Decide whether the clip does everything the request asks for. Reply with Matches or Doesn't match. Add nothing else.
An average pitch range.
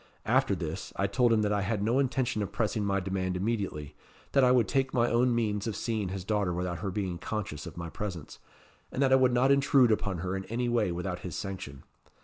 Matches